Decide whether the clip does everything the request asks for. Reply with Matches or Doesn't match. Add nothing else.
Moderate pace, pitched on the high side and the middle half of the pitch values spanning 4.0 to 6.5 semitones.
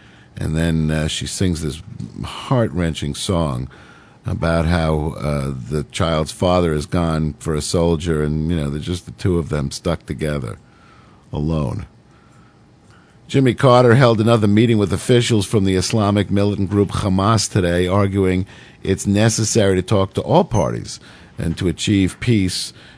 Doesn't match